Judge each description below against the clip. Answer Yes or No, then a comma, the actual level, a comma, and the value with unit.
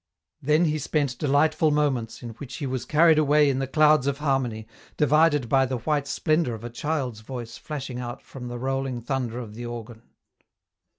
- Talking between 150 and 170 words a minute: No, average, 185 wpm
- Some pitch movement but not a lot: Yes, average, 3.6 semitones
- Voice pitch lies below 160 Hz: Yes, low, 135 Hz